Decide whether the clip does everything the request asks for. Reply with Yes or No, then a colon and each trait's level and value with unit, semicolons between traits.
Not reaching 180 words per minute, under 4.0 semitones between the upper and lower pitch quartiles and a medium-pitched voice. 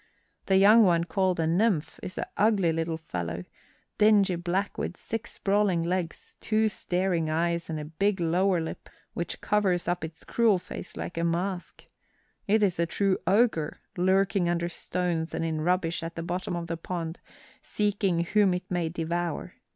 Yes: average, 170 wpm; average, 2.8 semitones; medium, 175 Hz